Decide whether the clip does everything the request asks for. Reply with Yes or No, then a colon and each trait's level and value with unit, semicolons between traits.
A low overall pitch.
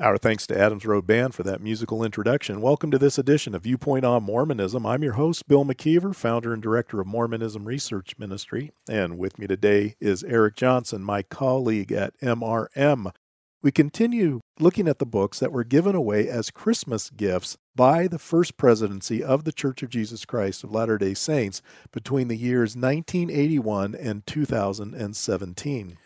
Yes: low, 115 Hz